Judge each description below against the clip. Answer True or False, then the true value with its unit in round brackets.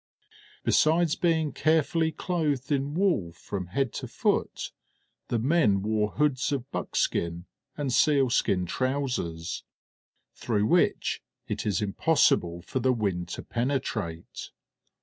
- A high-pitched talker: False (130 Hz)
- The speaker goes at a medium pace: False (115 wpm)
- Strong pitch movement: True (7.2 semitones)